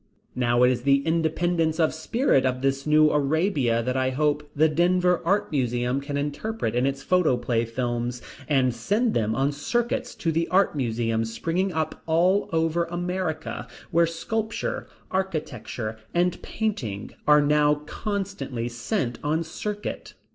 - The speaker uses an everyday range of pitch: No, wide, 5.7 semitones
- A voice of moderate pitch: Yes, medium, 150 Hz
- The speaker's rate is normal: Yes, average, 145 wpm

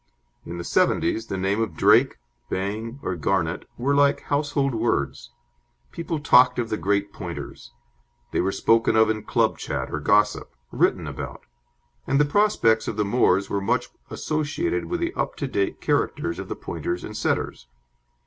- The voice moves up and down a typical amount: No, wide, 6.4 semitones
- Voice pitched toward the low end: Yes, low, 110 Hz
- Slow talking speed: No, average, 170 wpm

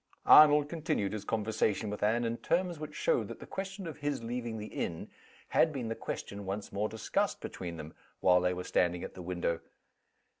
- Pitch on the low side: Yes, low, 110 Hz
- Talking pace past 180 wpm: Yes, average, 195 wpm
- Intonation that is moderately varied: No, wide, 7.7 semitones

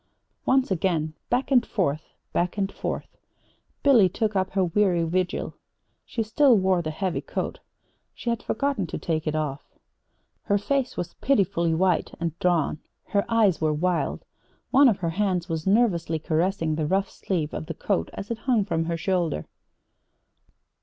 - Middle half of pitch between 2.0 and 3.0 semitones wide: No, average, 4.2 semitones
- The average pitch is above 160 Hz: Yes, medium, 185 Hz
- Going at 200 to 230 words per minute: No, average, 165 wpm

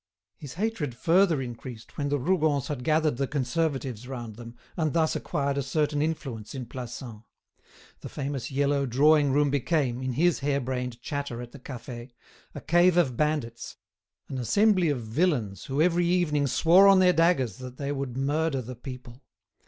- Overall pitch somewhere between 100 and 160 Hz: Yes, medium, 140 Hz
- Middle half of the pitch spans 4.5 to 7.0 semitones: No, average, 4.0 semitones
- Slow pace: No, average, 170 wpm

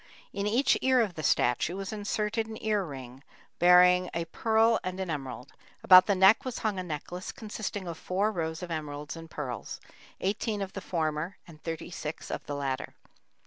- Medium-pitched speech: Yes, medium, 180 Hz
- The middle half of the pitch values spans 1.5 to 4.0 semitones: No, average, 4.9 semitones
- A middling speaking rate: Yes, average, 185 wpm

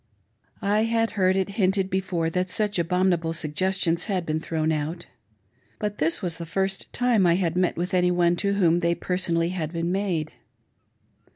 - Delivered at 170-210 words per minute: Yes, average, 185 wpm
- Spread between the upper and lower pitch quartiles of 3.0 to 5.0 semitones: No, narrow, 2.5 semitones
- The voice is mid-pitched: Yes, medium, 180 Hz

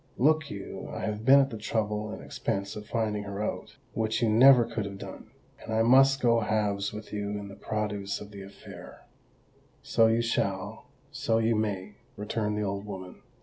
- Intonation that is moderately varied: No, narrow, 2.0 semitones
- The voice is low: Yes, low, 105 Hz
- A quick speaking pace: No, average, 175 wpm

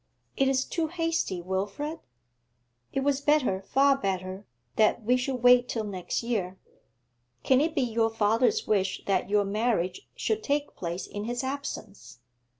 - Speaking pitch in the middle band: No, high, 240 Hz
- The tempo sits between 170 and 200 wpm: No, average, 150 wpm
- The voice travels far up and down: Yes, wide, 5.9 semitones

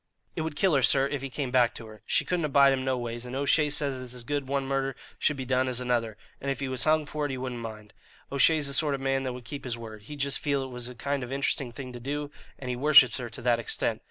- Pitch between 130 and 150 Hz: Yes, low, 135 Hz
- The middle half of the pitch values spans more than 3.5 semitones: No, narrow, 2.4 semitones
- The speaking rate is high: Yes, fast, 295 wpm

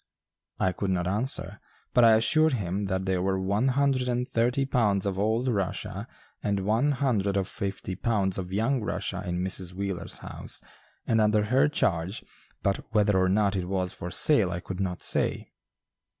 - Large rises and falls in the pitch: No, average, 3.7 semitones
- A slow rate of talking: No, average, 180 wpm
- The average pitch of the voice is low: Yes, low, 100 Hz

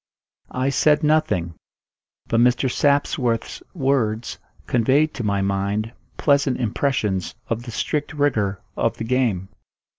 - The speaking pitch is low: Yes, low, 120 Hz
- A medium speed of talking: No, slow, 120 wpm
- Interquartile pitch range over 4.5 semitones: Yes, average, 4.9 semitones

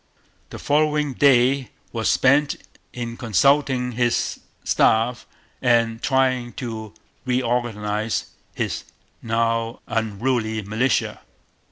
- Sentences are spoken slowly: Yes, slow, 85 wpm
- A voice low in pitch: Yes, low, 120 Hz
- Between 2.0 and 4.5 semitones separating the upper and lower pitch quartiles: Yes, narrow, 2.5 semitones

